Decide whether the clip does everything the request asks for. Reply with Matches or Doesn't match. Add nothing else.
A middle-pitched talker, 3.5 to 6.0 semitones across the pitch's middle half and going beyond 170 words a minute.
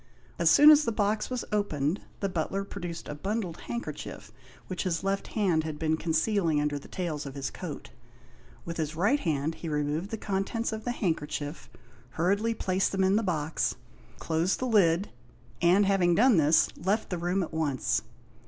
Matches